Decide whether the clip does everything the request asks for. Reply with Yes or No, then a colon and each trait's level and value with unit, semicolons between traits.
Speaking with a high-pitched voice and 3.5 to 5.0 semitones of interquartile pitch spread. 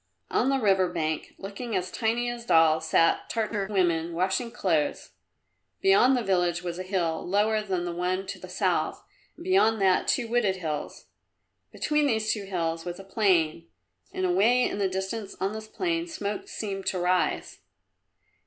Yes: high, 195 Hz; average, 4.0 semitones